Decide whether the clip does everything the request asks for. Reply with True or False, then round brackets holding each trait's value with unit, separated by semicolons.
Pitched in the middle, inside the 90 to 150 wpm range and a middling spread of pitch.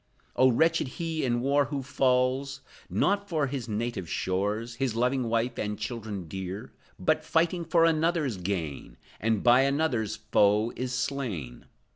False (125 Hz; 145 wpm; 4.8 semitones)